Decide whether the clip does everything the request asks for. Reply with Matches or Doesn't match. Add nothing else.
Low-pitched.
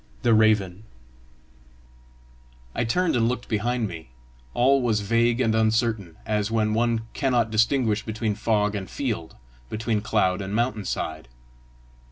Matches